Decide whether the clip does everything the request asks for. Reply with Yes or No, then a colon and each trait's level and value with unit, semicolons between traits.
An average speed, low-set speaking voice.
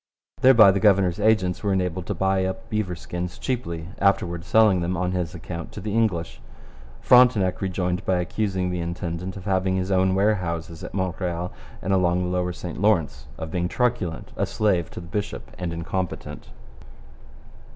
Yes: average, 170 wpm; very low, 90 Hz